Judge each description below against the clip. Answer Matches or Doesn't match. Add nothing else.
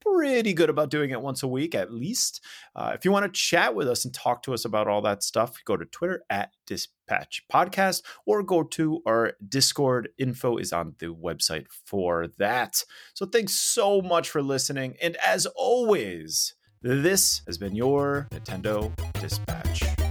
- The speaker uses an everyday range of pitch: Doesn't match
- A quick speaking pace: Doesn't match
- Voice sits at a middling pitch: Doesn't match